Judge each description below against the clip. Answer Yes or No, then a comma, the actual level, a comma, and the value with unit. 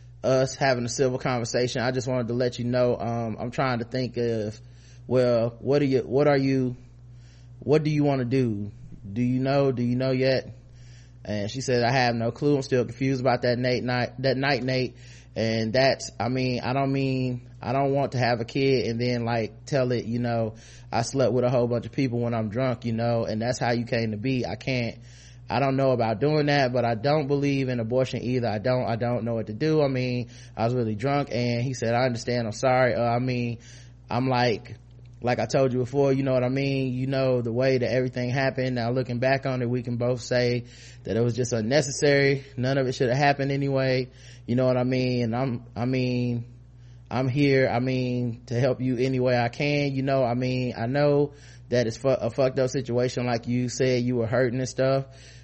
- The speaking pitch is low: Yes, low, 125 Hz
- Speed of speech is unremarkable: No, fast, 235 wpm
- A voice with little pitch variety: Yes, narrow, 1.6 semitones